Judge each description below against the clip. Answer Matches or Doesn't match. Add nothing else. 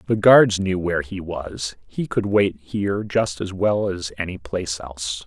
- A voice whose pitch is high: Doesn't match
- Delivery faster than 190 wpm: Doesn't match